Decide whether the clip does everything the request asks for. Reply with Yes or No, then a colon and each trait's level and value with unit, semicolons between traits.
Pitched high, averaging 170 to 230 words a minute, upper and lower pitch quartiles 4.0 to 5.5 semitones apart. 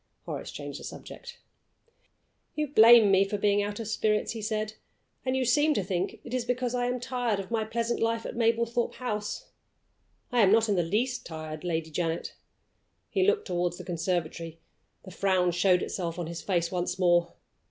Yes: high, 205 Hz; average, 185 wpm; average, 5.0 semitones